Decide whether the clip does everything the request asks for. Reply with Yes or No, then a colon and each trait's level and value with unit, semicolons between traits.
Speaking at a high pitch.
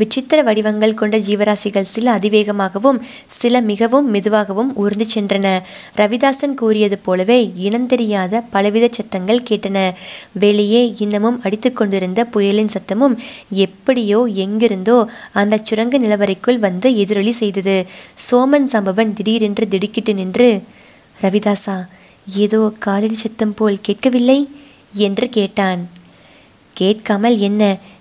Yes: high, 215 Hz